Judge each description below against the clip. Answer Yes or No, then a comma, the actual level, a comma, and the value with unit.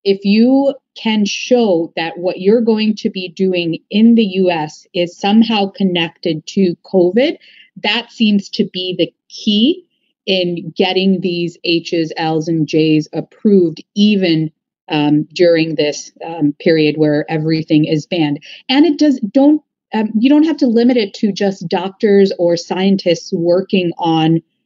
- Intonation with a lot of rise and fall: No, average, 4.6 semitones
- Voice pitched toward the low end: No, high, 190 Hz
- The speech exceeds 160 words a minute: No, average, 150 wpm